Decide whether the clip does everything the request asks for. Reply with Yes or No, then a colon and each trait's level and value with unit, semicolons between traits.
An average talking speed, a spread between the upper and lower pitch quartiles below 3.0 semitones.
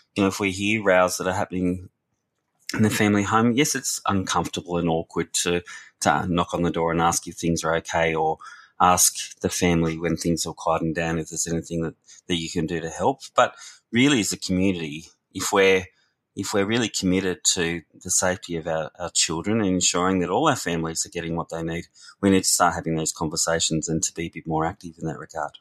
No: fast, 225 wpm; narrow, 2.5 semitones